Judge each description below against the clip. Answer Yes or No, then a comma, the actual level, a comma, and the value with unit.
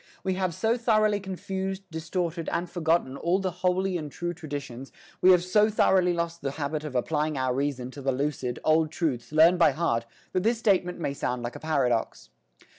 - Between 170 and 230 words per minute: Yes, average, 190 wpm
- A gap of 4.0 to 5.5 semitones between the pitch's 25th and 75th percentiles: Yes, average, 4.6 semitones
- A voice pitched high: No, medium, 165 Hz